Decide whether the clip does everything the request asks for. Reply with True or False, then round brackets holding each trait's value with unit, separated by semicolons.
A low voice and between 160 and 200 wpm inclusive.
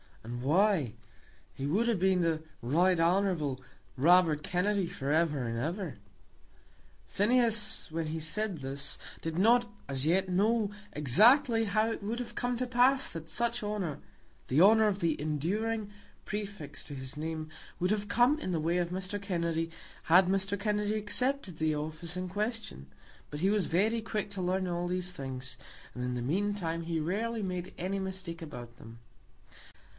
False (180 Hz; 165 wpm)